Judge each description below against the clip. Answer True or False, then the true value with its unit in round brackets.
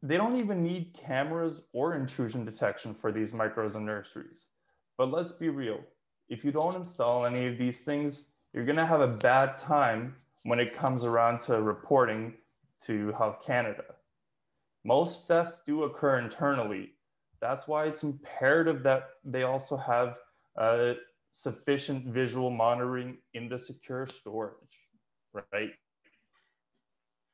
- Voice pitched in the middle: False (130 Hz)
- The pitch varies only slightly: False (3.7 semitones)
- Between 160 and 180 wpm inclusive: False (135 wpm)